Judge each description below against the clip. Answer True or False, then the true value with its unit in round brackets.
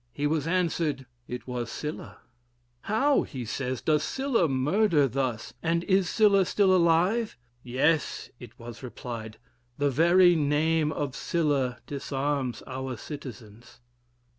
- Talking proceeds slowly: True (125 wpm)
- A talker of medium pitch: True (145 Hz)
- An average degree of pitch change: True (4.9 semitones)